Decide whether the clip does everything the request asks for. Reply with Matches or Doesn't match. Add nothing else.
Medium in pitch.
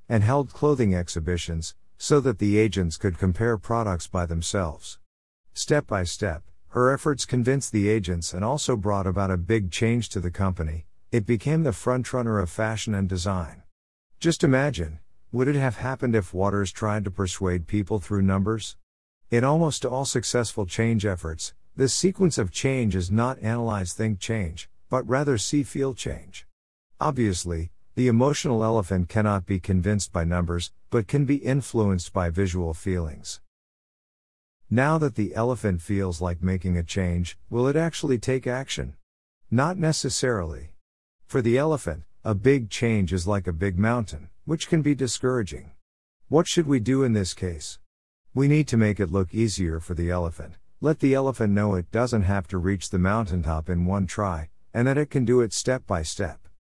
Doesn't match